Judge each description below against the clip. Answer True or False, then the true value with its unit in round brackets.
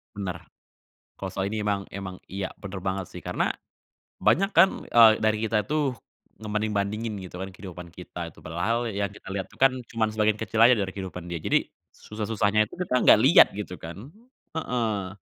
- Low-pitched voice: True (105 Hz)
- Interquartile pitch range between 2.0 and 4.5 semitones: True (2.9 semitones)